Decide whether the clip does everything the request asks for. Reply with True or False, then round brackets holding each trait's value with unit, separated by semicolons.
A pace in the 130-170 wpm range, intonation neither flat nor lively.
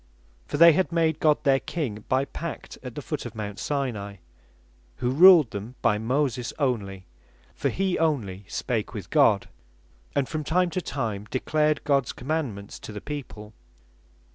False (160 wpm; 6.2 semitones)